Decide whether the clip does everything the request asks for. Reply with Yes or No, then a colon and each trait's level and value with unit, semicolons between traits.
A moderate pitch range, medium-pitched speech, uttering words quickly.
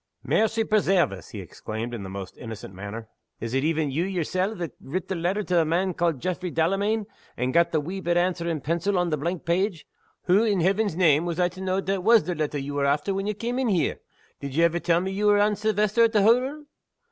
Yes: average, 4.4 semitones; medium, 175 Hz; fast, 240 wpm